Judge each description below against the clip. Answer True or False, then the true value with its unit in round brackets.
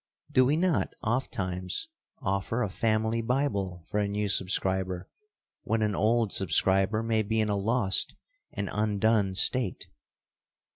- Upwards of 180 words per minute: False (135 wpm)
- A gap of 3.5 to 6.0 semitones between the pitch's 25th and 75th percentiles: False (2.8 semitones)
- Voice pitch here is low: True (105 Hz)